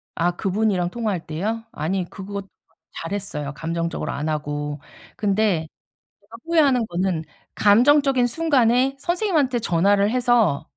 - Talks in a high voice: Yes, high, 205 Hz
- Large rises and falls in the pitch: Yes, wide, 6.5 semitones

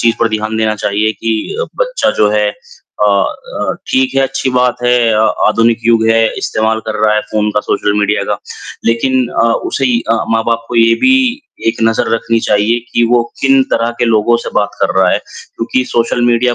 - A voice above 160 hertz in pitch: No, low, 115 Hz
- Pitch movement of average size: No, narrow, 2.1 semitones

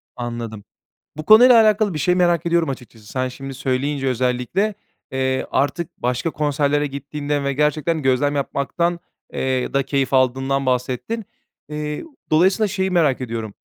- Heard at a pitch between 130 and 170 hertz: Yes, medium, 140 Hz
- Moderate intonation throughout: Yes, average, 4.5 semitones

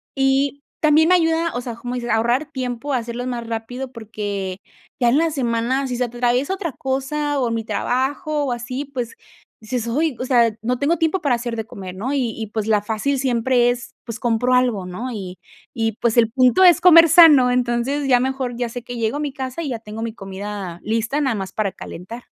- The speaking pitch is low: No, high, 245 Hz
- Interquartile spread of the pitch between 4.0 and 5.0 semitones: No, average, 3.2 semitones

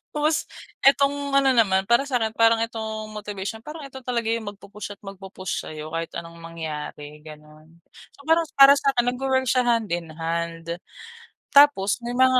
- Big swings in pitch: Yes, wide, 7.6 semitones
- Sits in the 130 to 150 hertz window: No, high, 220 Hz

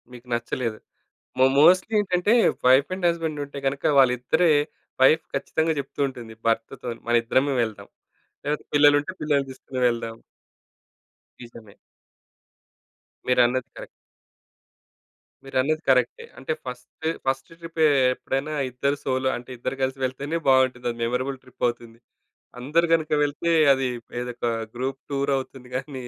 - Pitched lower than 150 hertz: Yes, low, 135 Hz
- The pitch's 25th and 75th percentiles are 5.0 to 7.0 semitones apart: No, average, 2.9 semitones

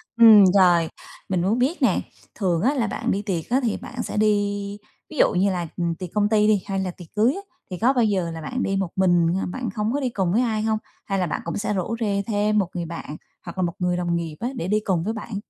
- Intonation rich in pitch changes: No, average, 3.7 semitones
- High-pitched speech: Yes, high, 200 Hz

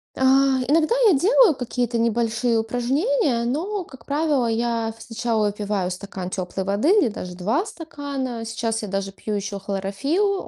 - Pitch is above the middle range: Yes, high, 235 Hz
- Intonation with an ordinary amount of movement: No, wide, 6.0 semitones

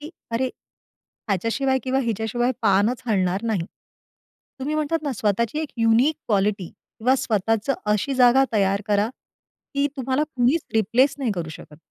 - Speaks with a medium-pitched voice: No, high, 230 Hz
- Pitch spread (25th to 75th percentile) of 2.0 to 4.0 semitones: No, average, 4.4 semitones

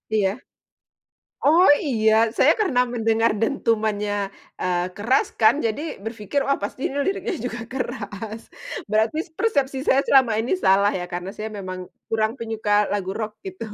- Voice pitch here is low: No, high, 225 Hz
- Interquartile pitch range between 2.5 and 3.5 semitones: No, average, 4.3 semitones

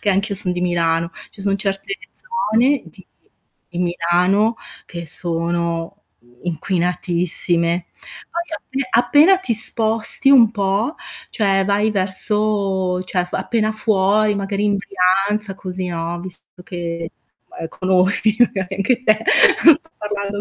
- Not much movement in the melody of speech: No, average, 3.2 semitones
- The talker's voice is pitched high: Yes, high, 195 Hz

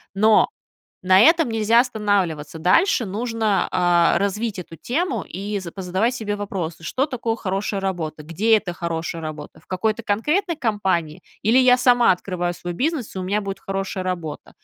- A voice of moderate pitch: No, high, 200 Hz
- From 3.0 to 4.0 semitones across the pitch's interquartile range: No, average, 4.4 semitones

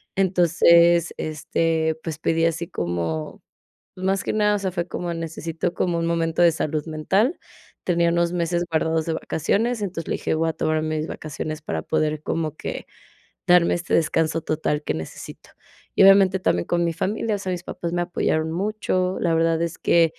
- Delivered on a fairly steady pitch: Yes, narrow, 2.0 semitones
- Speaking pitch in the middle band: Yes, medium, 165 Hz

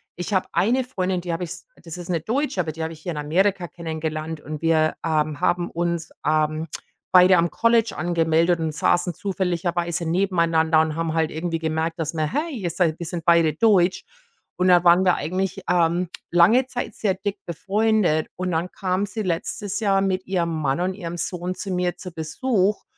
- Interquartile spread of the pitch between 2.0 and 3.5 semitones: Yes, narrow, 2.6 semitones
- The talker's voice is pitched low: No, medium, 175 Hz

